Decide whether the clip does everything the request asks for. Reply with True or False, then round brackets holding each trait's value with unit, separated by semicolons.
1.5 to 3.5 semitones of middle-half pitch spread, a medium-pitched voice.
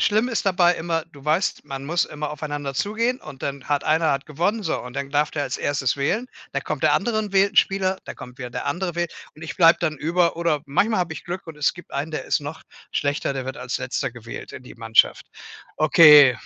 False (4.2 semitones; 155 Hz)